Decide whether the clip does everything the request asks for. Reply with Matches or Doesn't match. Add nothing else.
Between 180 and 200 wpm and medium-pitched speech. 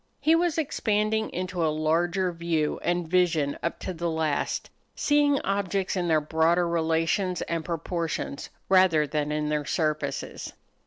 Doesn't match